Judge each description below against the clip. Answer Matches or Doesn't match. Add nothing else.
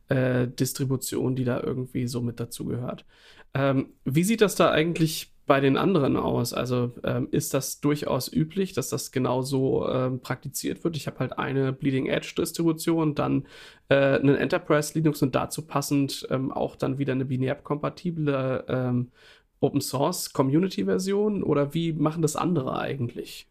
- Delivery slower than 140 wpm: Doesn't match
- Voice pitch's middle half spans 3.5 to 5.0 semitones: Doesn't match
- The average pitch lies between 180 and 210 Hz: Doesn't match